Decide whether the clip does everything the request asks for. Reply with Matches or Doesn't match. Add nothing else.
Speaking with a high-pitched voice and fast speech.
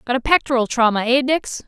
Matches